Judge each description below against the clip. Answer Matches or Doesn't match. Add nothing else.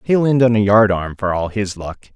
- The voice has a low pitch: Matches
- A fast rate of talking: Matches